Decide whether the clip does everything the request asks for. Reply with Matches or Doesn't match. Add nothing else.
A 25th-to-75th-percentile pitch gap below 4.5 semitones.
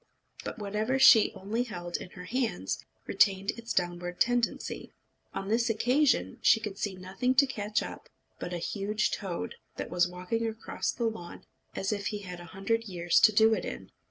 Matches